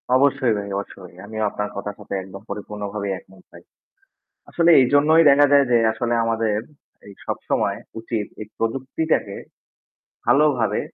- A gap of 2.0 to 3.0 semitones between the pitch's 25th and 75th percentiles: No, average, 5.1 semitones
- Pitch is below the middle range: Yes, low, 110 Hz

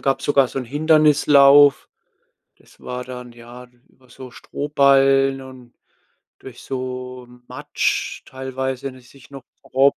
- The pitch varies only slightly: Yes, narrow, 1.4 semitones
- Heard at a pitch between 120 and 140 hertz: Yes, low, 130 Hz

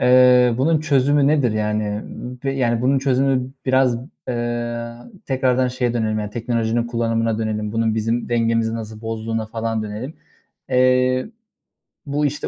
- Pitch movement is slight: Yes, narrow, 2.3 semitones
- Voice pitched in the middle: No, low, 120 Hz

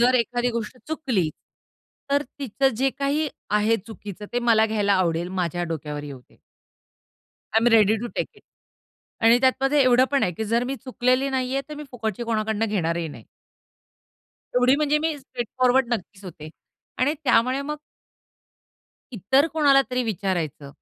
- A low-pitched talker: No, high, 240 Hz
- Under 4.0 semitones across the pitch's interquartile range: No, average, 4.8 semitones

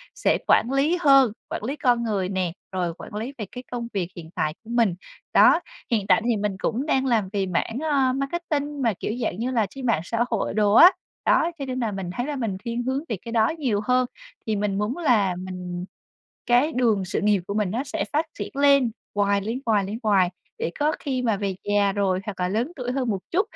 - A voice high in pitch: Yes, high, 225 Hz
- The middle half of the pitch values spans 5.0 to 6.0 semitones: No, average, 4.6 semitones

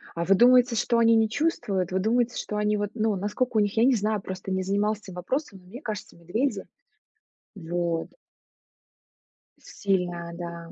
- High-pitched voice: Yes, high, 205 Hz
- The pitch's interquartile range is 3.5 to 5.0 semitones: Yes, average, 4.0 semitones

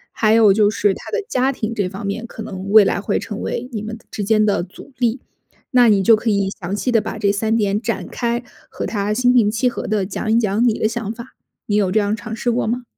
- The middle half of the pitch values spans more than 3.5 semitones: No, narrow, 2.5 semitones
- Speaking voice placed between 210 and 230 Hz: Yes, high, 215 Hz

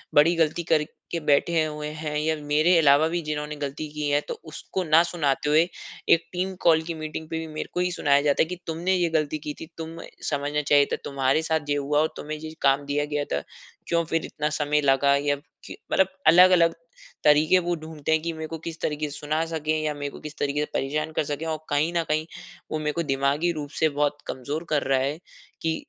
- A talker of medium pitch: Yes, medium, 155 Hz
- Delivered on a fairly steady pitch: Yes, narrow, 1.8 semitones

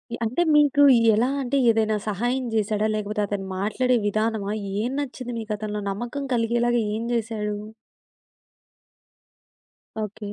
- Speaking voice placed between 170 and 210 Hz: No, high, 220 Hz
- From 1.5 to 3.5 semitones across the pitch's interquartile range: Yes, narrow, 2.5 semitones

